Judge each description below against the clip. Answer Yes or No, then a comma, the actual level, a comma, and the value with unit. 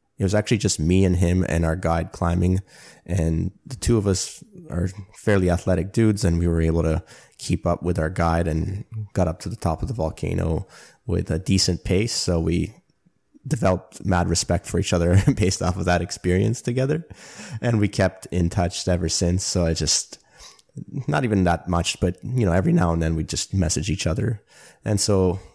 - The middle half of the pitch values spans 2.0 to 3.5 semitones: Yes, average, 2.9 semitones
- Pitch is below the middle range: Yes, very low, 90 Hz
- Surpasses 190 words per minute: Yes, average, 200 wpm